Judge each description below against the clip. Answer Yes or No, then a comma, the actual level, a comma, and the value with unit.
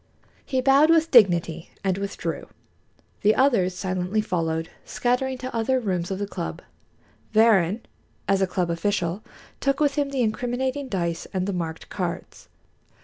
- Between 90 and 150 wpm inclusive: Yes, average, 145 wpm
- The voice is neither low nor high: No, high, 205 Hz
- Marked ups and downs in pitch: Yes, wide, 6.2 semitones